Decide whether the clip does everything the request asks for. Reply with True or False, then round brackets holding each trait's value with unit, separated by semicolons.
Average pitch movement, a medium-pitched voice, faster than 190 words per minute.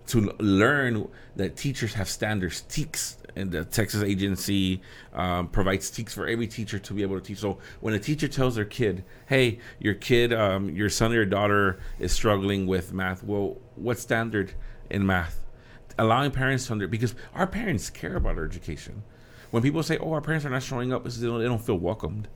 False (4.0 semitones; 105 Hz; 200 wpm)